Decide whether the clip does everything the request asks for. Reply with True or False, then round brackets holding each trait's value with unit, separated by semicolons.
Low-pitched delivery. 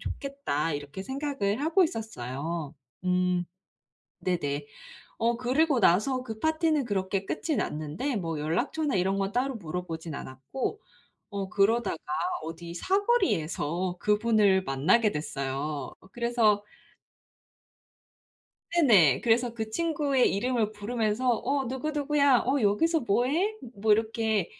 False (215 Hz)